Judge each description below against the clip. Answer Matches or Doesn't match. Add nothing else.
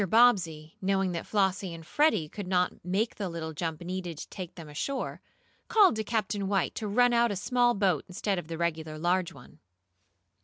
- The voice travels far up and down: Doesn't match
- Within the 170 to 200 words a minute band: Matches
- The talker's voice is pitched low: Doesn't match